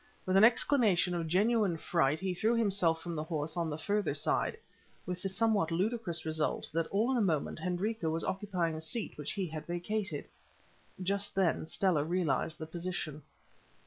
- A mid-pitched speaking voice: Yes, medium, 180 Hz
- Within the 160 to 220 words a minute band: Yes, average, 175 wpm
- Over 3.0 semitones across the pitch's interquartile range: Yes, average, 4.0 semitones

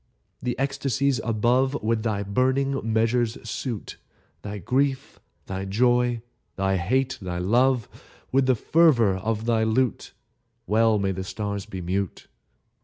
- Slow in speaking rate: Yes, slow, 130 wpm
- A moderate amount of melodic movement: Yes, average, 4.3 semitones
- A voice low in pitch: Yes, low, 115 Hz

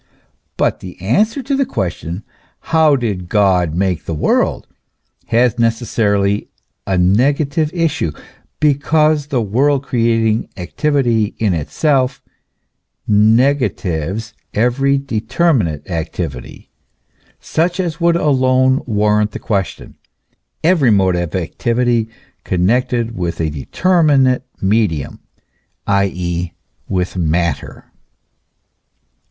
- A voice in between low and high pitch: No, low, 115 Hz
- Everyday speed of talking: No, slow, 95 wpm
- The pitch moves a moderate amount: No, wide, 7.0 semitones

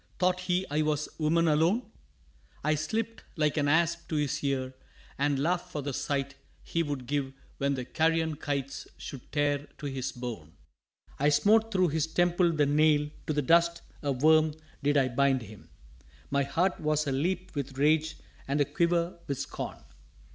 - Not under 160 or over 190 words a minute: Yes, average, 175 wpm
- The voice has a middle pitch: Yes, medium, 150 Hz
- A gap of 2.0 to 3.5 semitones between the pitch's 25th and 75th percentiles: Yes, average, 3.2 semitones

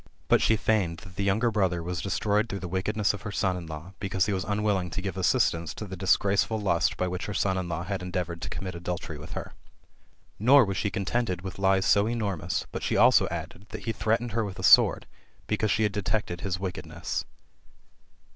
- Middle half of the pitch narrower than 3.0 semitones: Yes, narrow, 2.6 semitones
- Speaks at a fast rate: Yes, fast, 220 wpm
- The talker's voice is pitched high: No, very low, 95 Hz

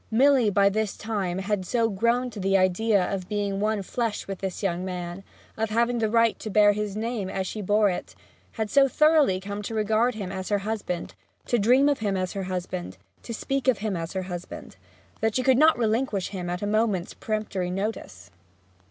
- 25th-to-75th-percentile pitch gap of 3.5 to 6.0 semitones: No, average, 3.1 semitones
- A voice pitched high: Yes, high, 210 Hz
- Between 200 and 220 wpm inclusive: Yes, fast, 205 wpm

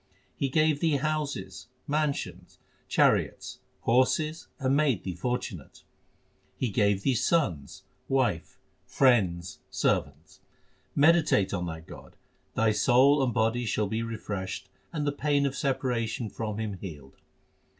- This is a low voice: Yes, low, 120 Hz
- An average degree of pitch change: No, wide, 6.4 semitones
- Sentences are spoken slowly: Yes, slow, 130 wpm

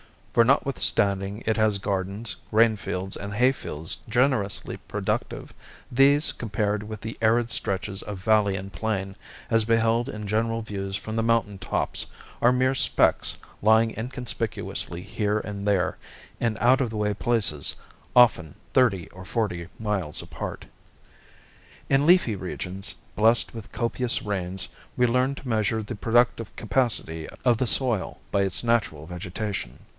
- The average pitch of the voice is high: No, low, 110 Hz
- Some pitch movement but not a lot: Yes, average, 3.1 semitones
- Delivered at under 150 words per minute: Yes, average, 140 wpm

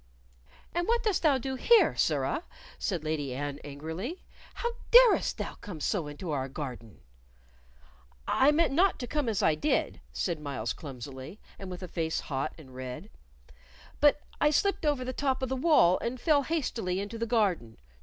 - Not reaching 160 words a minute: No, average, 175 wpm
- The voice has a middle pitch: No, high, 200 Hz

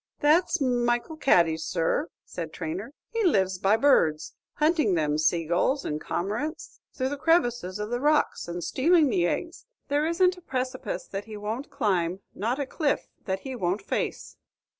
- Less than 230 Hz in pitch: No, high, 240 Hz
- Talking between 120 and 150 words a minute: No, average, 160 wpm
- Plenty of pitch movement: Yes, wide, 8.3 semitones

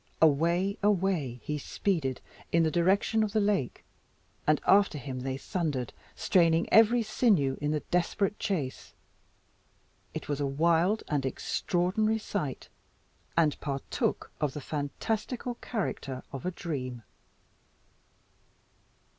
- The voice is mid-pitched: Yes, medium, 165 Hz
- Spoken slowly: Yes, slow, 115 wpm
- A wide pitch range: Yes, wide, 6.2 semitones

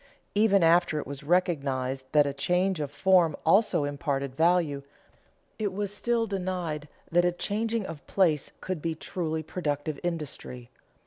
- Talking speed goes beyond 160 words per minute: No, average, 145 wpm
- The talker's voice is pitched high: No, medium, 165 Hz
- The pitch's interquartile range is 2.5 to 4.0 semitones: No, average, 4.4 semitones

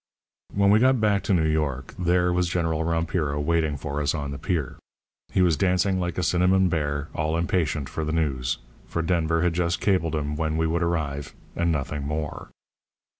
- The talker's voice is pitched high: No, very low, 80 Hz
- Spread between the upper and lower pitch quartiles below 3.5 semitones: Yes, average, 2.9 semitones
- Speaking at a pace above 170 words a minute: Yes, average, 190 wpm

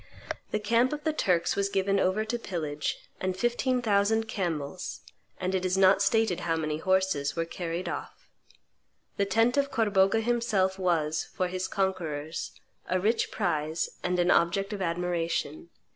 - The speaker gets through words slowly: No, average, 160 wpm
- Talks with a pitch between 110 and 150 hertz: No, high, 190 Hz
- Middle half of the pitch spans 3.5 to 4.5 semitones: Yes, average, 3.9 semitones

